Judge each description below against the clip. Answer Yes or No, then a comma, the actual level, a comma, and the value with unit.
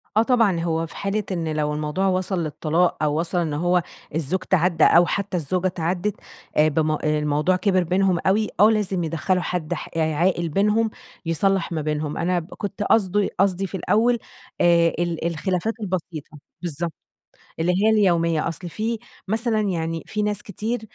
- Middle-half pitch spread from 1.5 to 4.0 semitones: Yes, average, 3.4 semitones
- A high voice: No, medium, 180 Hz